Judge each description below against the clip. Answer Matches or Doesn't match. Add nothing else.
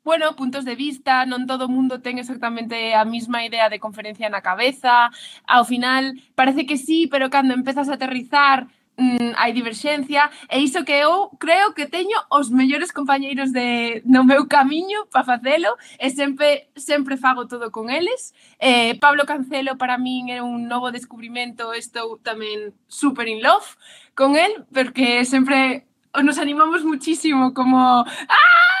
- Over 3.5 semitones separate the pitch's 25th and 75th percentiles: Doesn't match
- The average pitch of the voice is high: Matches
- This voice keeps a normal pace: Matches